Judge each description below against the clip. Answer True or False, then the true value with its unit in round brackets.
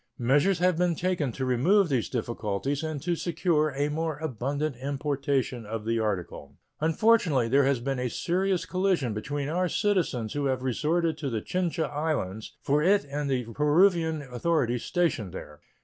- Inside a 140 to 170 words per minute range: True (165 wpm)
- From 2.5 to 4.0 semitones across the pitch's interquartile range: False (5.1 semitones)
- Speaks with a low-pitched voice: False (145 Hz)